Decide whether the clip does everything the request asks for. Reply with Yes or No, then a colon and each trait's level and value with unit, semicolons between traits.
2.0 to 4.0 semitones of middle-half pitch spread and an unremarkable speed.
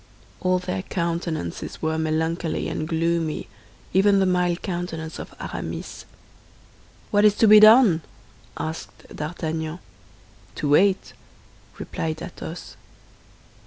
No: average, 2.7 semitones; slow, 105 wpm